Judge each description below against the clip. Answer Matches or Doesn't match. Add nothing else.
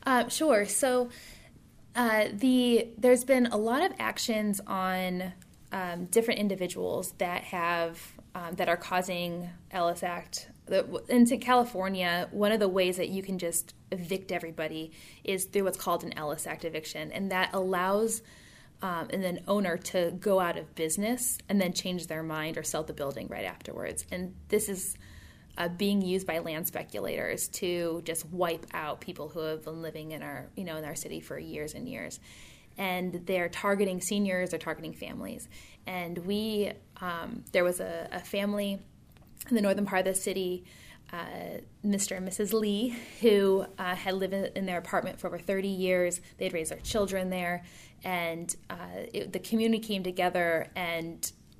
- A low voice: Doesn't match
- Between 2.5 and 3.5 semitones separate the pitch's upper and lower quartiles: Matches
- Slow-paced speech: Doesn't match